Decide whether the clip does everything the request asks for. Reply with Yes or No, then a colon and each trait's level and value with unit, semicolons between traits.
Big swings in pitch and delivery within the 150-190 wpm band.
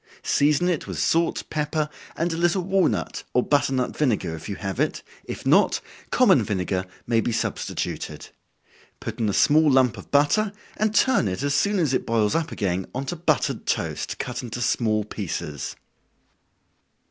Yes: wide, 7.3 semitones; average, 170 wpm